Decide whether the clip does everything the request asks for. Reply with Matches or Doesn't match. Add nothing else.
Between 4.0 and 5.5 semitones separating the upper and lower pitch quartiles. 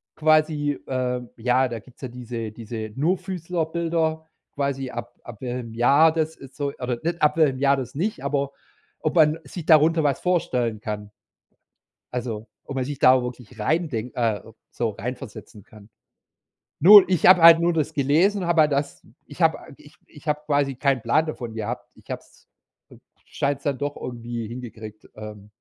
Matches